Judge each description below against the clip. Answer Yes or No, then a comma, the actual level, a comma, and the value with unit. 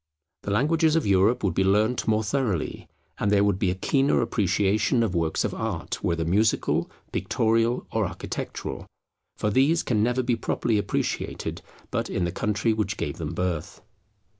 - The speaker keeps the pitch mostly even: No, average, 4.0 semitones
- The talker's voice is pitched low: Yes, low, 105 Hz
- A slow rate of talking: No, average, 165 wpm